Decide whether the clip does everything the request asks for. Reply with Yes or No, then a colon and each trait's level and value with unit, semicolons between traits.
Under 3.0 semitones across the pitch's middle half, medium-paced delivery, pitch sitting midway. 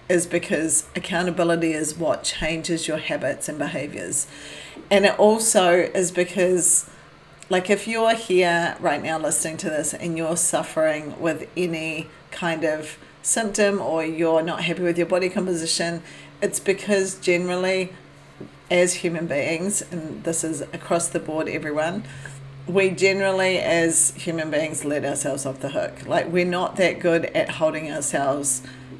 Yes: narrow, 2.5 semitones; average, 145 wpm; medium, 170 Hz